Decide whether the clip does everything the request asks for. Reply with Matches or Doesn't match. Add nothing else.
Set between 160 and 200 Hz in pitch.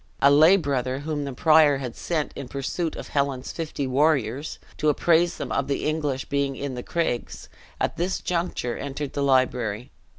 Doesn't match